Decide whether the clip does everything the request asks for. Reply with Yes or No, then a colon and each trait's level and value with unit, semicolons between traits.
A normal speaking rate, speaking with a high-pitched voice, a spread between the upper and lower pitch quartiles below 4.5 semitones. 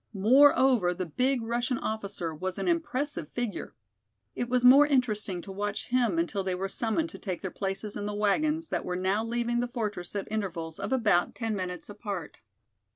No: average, 185 wpm; high, 210 Hz; average, 4.8 semitones